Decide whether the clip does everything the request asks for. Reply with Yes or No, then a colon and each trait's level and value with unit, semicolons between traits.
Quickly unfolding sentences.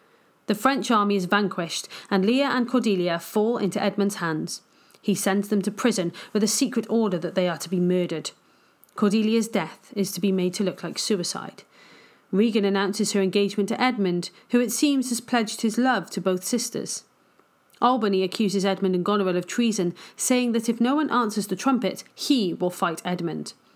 No: average, 185 wpm